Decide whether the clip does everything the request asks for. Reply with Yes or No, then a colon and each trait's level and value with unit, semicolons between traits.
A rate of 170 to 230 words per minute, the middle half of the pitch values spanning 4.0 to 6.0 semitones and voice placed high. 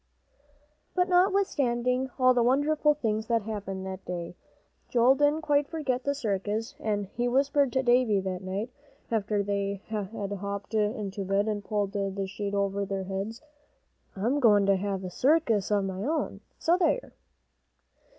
No: average, 155 wpm; average, 4.8 semitones; high, 215 Hz